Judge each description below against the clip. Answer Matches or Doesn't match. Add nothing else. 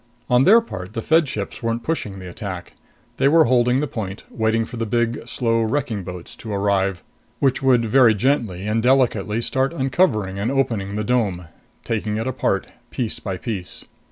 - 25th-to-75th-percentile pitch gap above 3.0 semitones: Matches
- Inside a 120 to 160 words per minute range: Doesn't match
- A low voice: Matches